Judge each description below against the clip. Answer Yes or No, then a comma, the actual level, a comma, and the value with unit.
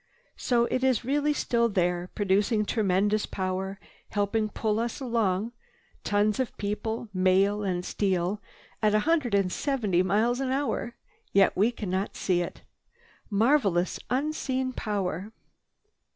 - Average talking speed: No, slow, 125 wpm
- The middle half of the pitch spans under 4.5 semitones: Yes, average, 4.0 semitones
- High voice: Yes, high, 210 Hz